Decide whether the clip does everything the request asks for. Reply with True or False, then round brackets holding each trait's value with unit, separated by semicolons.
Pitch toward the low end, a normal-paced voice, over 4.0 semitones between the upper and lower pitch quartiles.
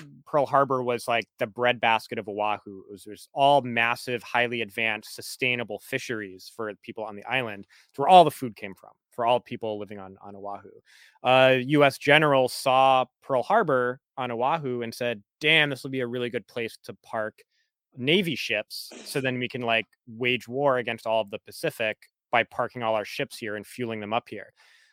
False (120 Hz; 195 wpm; 3.2 semitones)